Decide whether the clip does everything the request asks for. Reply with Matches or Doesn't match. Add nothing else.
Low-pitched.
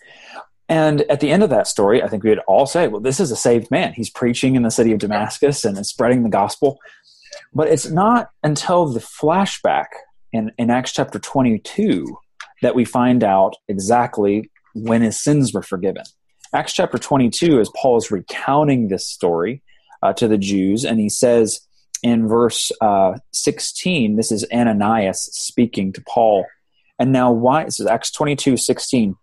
Matches